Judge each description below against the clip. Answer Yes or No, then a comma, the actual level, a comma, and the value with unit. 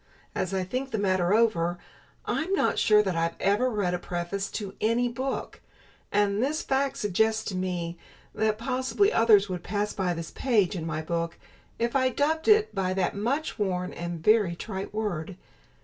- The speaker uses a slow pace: No, average, 180 wpm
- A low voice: No, high, 205 Hz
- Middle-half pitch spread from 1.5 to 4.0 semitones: No, average, 4.8 semitones